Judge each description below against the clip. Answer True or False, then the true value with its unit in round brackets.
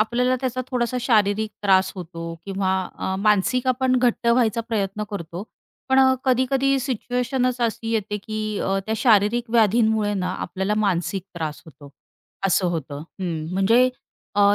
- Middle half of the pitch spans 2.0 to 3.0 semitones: False (4.3 semitones)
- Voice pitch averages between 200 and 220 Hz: True (215 Hz)